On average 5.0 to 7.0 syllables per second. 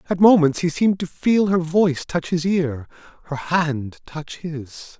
No: 4.3 syllables/s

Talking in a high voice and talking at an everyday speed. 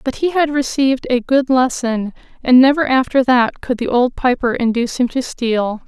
Yes: very high, 255 Hz; average, 195 wpm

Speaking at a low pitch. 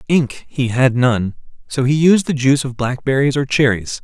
Yes: low, 130 Hz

